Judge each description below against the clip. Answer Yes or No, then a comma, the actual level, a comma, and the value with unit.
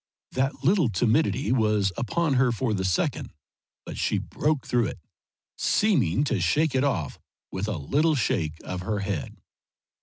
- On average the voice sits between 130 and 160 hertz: No, low, 120 Hz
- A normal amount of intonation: No, wide, 6.5 semitones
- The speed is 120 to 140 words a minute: No, average, 155 wpm